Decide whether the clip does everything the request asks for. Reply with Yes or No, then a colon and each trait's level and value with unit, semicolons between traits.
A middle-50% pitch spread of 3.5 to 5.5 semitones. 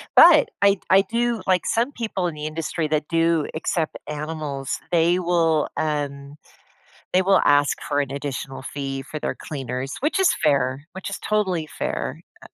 Yes: average, 4.6 semitones